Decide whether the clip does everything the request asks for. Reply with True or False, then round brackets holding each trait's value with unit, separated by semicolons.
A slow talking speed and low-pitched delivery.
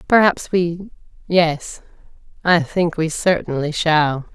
False (95 wpm; 165 Hz)